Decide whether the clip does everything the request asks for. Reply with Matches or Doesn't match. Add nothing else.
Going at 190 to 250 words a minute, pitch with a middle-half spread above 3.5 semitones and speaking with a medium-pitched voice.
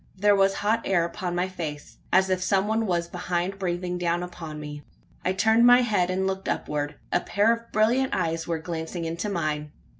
Doesn't match